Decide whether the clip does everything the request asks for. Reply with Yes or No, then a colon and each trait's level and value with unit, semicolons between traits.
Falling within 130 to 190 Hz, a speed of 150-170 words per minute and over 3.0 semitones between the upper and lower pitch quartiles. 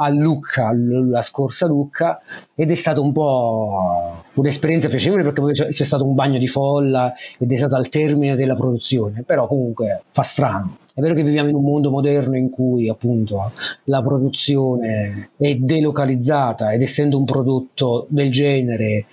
No: low, 135 Hz; average, 165 wpm; average, 2.7 semitones